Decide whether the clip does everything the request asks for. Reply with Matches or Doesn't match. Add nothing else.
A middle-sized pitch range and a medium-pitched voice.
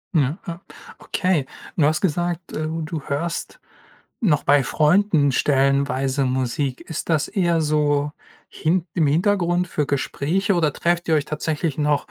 Matches